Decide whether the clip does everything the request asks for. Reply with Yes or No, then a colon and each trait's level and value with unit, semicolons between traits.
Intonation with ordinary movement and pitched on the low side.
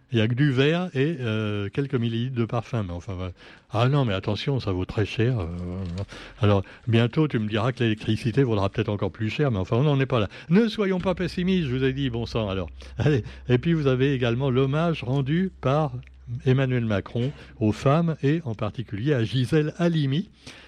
Yes: average, 4.8 semitones; low, 125 Hz